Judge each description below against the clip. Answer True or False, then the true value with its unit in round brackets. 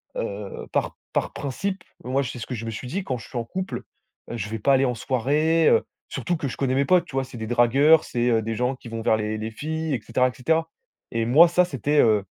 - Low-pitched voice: True (130 Hz)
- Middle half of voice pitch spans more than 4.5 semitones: True (5.2 semitones)